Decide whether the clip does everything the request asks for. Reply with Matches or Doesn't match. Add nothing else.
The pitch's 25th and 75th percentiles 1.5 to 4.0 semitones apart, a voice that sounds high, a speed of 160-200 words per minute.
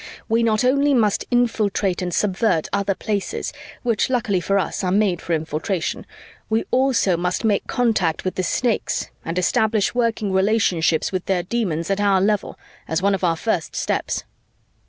Matches